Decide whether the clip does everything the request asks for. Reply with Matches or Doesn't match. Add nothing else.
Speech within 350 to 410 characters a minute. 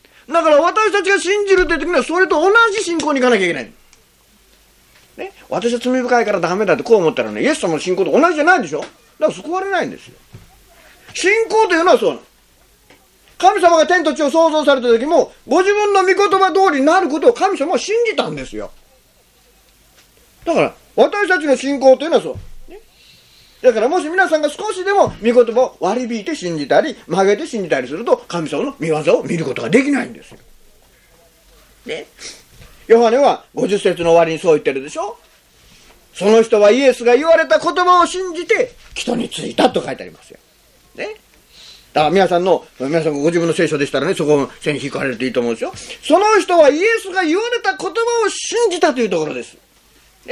Matches